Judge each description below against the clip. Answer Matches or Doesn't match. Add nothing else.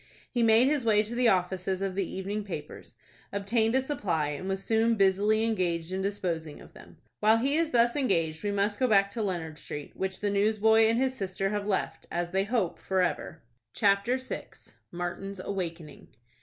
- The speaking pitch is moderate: Doesn't match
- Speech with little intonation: Doesn't match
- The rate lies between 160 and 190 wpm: Matches